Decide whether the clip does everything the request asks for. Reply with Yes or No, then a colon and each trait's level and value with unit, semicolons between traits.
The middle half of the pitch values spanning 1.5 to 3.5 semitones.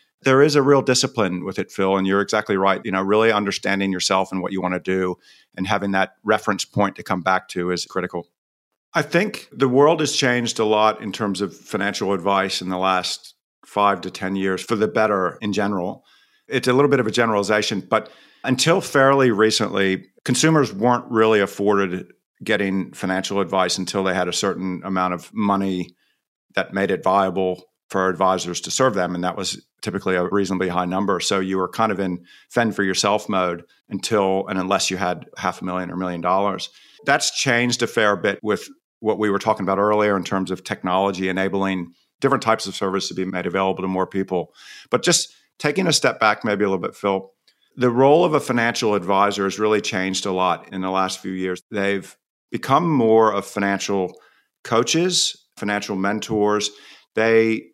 Yes: average, 2.7 semitones